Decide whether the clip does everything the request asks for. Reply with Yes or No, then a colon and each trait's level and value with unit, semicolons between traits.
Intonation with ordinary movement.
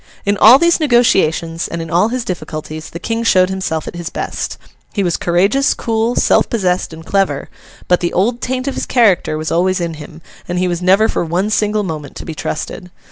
Yes: average, 4.9 semitones